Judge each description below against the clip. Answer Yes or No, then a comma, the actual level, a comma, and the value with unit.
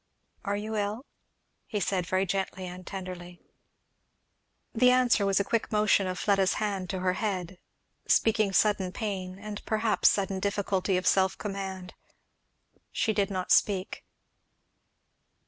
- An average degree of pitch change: No, narrow, 2.1 semitones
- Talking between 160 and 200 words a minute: No, slow, 135 wpm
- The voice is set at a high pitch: Yes, high, 195 Hz